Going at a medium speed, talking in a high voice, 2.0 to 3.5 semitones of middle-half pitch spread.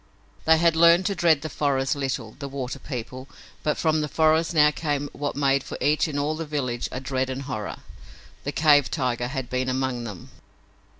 No: average, 195 wpm; medium, 140 Hz; average, 3.2 semitones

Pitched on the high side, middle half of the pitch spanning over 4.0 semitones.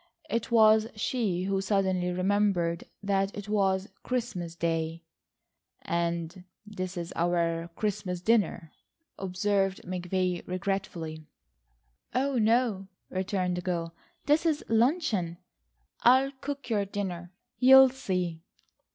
No: high, 195 Hz; average, 3.7 semitones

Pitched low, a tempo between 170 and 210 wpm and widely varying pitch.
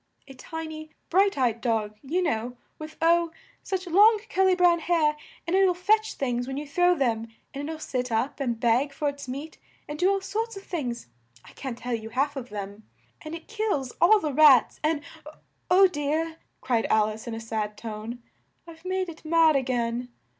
No: very high, 295 Hz; fast, 205 wpm; wide, 6.0 semitones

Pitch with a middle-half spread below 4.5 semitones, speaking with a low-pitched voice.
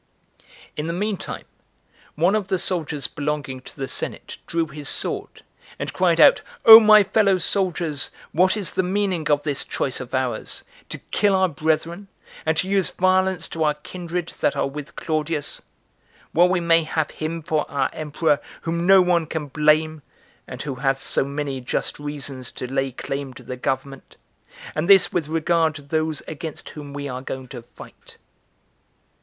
No: average, 3.8 semitones; medium, 155 Hz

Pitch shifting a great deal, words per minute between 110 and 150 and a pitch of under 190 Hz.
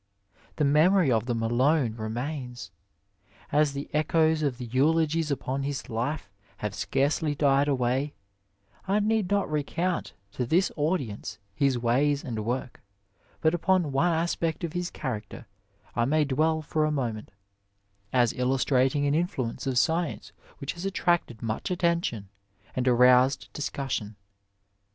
No: average, 4.3 semitones; average, 140 wpm; medium, 140 Hz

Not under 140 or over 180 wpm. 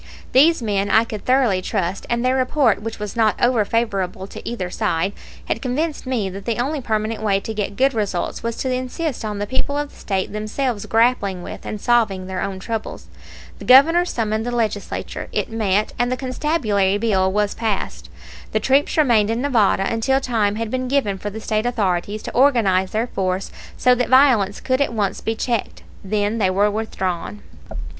No: average, 190 wpm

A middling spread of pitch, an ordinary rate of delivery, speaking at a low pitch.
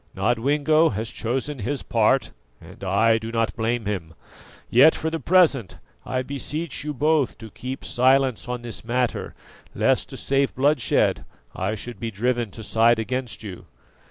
Yes: average, 3.6 semitones; average, 155 wpm; low, 120 Hz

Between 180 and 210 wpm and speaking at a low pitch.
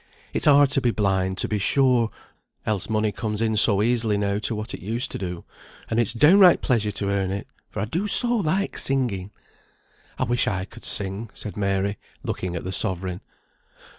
Yes: average, 195 wpm; low, 105 Hz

